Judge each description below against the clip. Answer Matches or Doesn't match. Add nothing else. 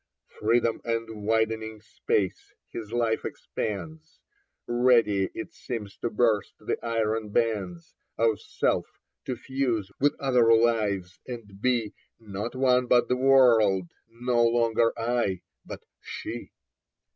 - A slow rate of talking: Matches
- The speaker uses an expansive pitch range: Doesn't match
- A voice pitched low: Matches